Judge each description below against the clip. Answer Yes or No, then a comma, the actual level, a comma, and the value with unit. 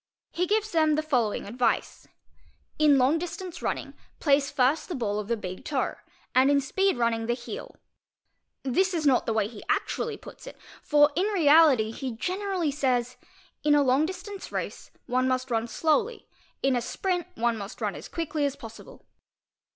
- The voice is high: Yes, very high, 280 Hz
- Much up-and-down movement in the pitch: Yes, wide, 6.0 semitones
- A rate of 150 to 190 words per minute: Yes, average, 175 wpm